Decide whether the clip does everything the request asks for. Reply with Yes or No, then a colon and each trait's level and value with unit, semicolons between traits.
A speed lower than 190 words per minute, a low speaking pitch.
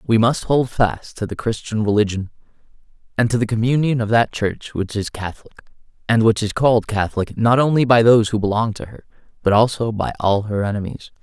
No: average, 200 wpm; low, 110 Hz